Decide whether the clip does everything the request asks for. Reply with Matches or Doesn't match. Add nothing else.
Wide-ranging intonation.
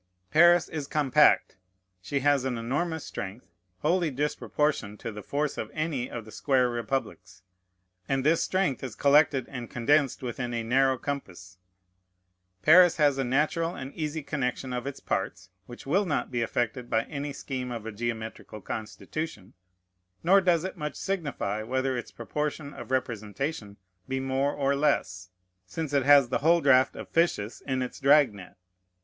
Doesn't match